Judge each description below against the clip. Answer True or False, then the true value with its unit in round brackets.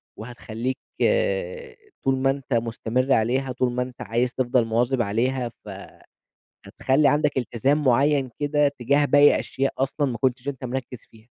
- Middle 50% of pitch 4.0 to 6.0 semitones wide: False (2.8 semitones)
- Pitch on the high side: False (130 Hz)